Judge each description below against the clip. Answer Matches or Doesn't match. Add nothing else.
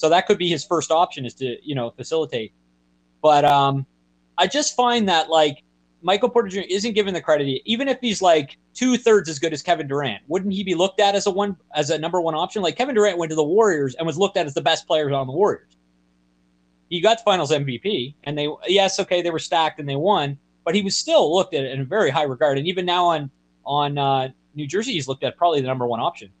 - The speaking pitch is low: Doesn't match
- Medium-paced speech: Doesn't match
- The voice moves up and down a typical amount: Doesn't match